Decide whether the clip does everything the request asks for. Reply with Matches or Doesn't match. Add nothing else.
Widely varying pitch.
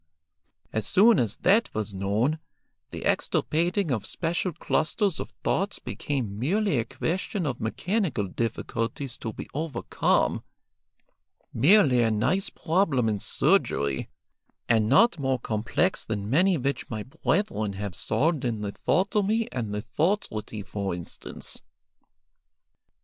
Matches